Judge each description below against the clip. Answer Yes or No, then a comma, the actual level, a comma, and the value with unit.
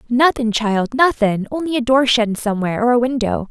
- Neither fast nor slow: Yes, average, 190 wpm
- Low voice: No, high, 240 Hz